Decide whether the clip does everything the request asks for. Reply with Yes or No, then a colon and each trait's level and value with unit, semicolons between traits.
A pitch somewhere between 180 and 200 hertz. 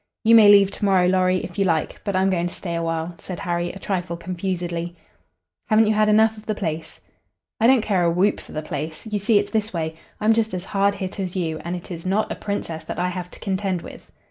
Yes: medium, 185 Hz